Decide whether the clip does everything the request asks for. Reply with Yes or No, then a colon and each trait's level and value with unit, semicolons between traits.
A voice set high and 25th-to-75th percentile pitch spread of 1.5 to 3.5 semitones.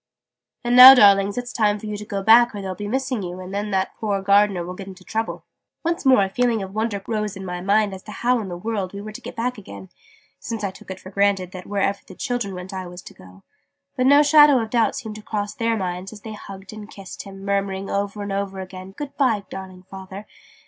Yes: high, 200 Hz; average, 2.7 semitones